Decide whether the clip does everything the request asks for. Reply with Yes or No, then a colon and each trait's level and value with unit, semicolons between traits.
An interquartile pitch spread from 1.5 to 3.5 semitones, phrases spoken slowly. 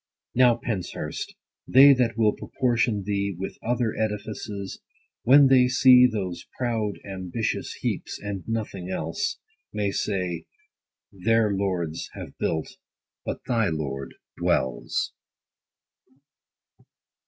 No: average, 4.1 semitones; slow, 110 wpm